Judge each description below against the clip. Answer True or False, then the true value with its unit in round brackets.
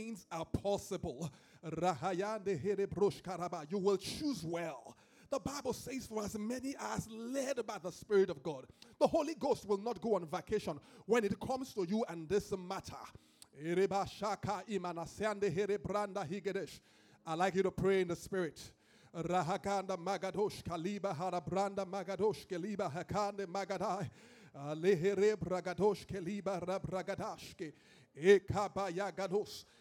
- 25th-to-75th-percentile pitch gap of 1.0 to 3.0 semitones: True (2.5 semitones)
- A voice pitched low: False (195 Hz)